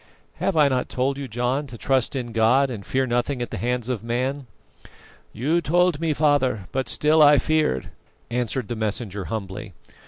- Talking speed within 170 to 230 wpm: Yes, average, 180 wpm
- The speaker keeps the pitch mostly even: No, average, 3.7 semitones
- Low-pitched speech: Yes, low, 125 Hz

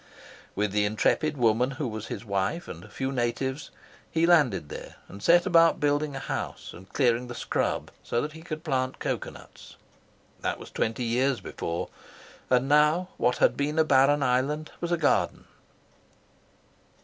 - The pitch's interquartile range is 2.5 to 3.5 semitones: No, average, 4.5 semitones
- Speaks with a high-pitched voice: No, low, 135 Hz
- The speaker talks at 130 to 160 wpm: No, average, 170 wpm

